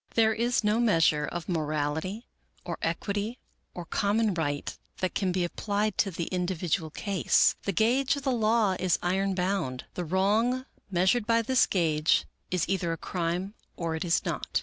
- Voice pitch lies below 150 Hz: No, high, 190 Hz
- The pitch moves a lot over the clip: No, average, 4.4 semitones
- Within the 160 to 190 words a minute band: Yes, average, 170 wpm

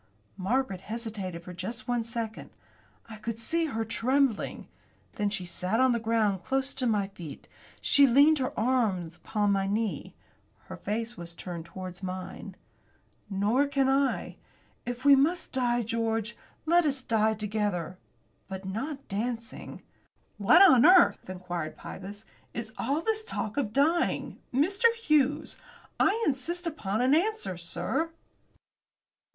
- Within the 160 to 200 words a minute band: No, average, 140 wpm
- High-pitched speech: Yes, high, 230 Hz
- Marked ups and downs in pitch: Yes, wide, 5.7 semitones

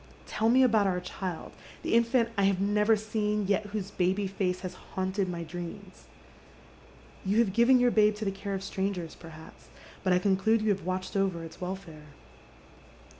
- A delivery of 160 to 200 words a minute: Yes, average, 175 wpm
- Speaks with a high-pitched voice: Yes, high, 195 Hz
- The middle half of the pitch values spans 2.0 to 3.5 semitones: Yes, narrow, 2.4 semitones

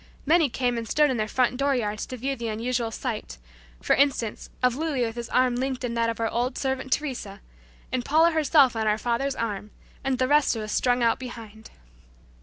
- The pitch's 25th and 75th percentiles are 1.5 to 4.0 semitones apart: Yes, average, 2.8 semitones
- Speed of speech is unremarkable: No, fast, 210 wpm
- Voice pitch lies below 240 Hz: No, high, 245 Hz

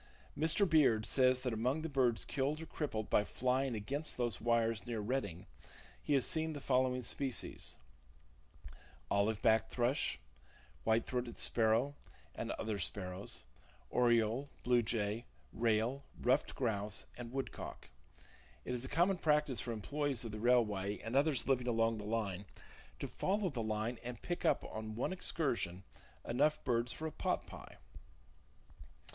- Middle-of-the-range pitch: No, low, 120 Hz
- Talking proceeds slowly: No, average, 150 wpm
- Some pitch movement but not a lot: Yes, average, 3.8 semitones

